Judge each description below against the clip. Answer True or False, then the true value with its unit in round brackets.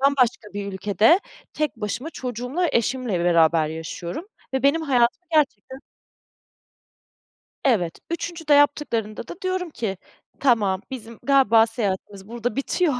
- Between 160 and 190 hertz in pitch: False (240 Hz)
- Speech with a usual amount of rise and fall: False (5.9 semitones)